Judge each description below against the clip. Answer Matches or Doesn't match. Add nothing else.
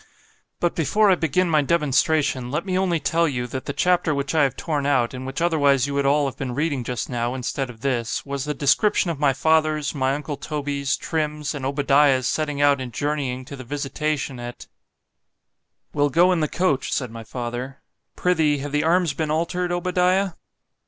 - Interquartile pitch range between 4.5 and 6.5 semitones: Doesn't match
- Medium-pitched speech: Matches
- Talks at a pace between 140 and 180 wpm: Doesn't match